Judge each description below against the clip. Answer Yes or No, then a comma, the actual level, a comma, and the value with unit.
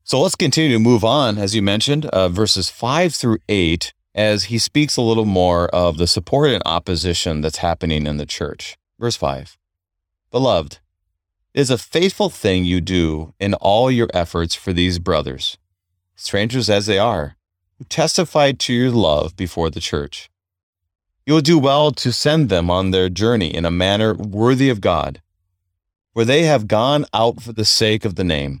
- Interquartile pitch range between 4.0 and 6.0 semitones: Yes, average, 5.1 semitones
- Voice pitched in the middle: No, very low, 95 Hz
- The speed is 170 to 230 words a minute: Yes, average, 180 wpm